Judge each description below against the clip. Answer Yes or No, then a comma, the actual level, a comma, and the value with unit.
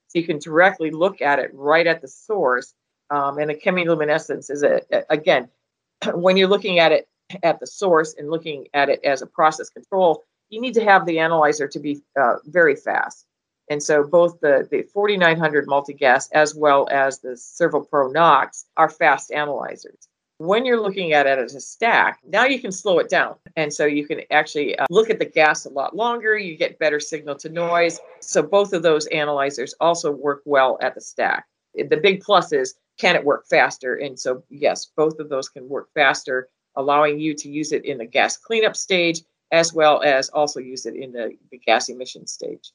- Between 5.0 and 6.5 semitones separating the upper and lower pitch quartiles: Yes, wide, 5.4 semitones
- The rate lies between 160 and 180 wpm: No, fast, 205 wpm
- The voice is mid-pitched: Yes, medium, 160 Hz